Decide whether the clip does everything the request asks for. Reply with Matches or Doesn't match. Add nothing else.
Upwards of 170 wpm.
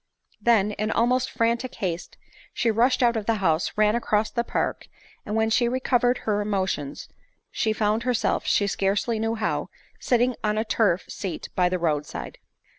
Matches